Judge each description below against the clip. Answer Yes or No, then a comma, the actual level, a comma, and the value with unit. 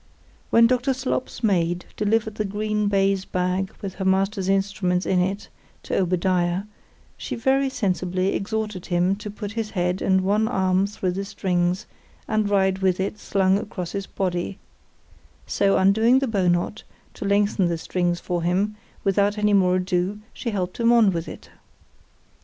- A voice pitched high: Yes, high, 195 Hz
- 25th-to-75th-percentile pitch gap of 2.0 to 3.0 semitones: Yes, narrow, 2.5 semitones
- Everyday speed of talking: Yes, average, 165 wpm